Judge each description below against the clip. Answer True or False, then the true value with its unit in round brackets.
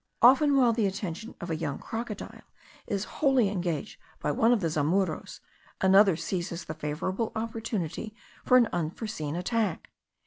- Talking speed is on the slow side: False (145 wpm)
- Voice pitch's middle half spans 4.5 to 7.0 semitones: True (5.2 semitones)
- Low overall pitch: False (195 Hz)